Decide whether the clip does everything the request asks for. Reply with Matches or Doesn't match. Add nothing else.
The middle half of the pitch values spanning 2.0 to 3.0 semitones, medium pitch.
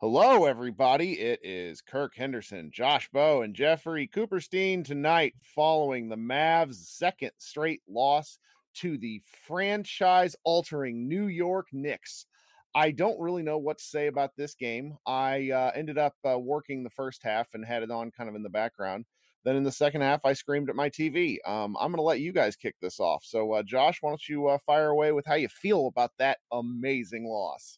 Doesn't match